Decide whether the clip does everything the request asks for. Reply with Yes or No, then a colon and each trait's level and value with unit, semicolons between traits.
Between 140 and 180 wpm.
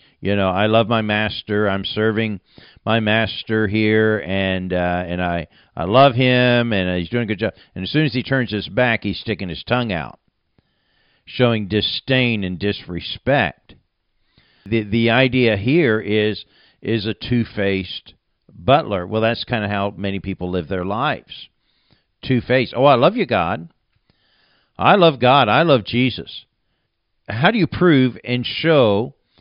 Yes: average, 165 wpm